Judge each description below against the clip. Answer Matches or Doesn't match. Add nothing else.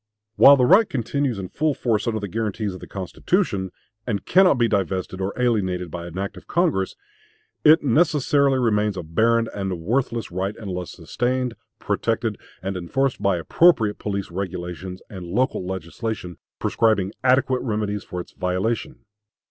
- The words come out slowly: Doesn't match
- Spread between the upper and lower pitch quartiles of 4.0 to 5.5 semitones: Matches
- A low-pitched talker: Matches